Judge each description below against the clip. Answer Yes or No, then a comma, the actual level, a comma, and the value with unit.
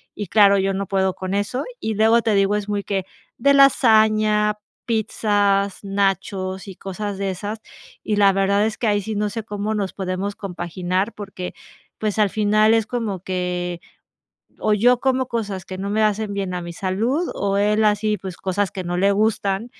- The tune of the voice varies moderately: No, narrow, 2.0 semitones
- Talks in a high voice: Yes, high, 205 Hz